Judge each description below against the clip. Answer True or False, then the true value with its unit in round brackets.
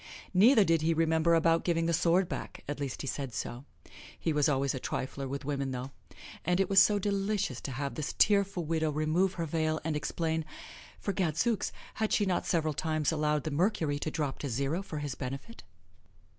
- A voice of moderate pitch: True (160 Hz)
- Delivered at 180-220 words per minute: True (200 wpm)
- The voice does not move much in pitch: False (3.8 semitones)